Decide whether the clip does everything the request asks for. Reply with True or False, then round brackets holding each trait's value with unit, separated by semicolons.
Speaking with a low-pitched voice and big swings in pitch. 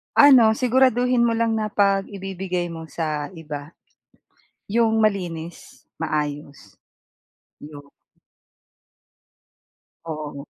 False (185 Hz; 6.4 semitones)